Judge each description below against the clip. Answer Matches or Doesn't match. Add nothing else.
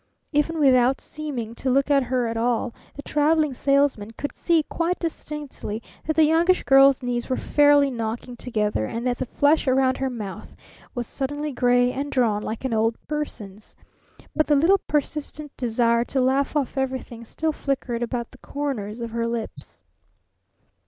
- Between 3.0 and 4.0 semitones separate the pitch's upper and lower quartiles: Matches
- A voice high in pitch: Matches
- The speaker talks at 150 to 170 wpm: Matches